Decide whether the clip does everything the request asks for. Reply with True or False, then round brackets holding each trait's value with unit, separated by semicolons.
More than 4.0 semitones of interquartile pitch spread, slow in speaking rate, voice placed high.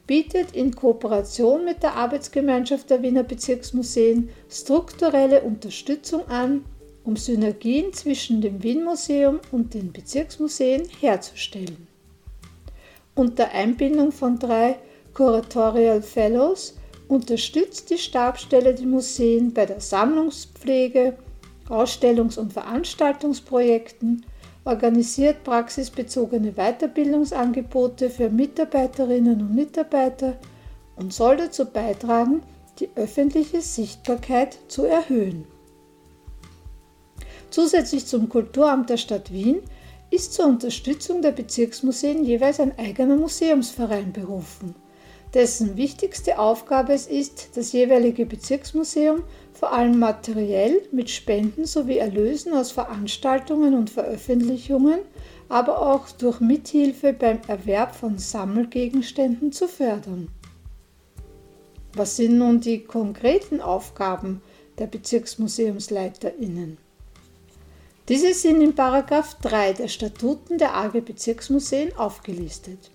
True (4.5 semitones; 95 wpm; 245 Hz)